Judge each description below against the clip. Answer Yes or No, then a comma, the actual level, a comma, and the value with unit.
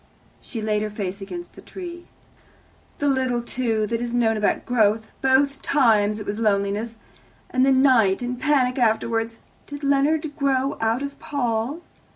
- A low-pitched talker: No, high, 240 Hz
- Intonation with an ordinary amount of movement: Yes, average, 4.1 semitones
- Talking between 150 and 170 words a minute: Yes, average, 160 wpm